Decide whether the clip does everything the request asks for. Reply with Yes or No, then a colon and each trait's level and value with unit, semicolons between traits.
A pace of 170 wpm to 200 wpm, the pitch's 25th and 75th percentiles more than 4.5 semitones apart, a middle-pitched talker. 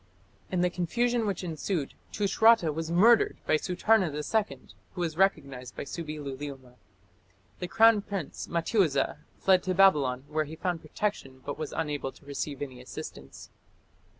No: average, 150 wpm; average, 5.2 semitones; medium, 165 Hz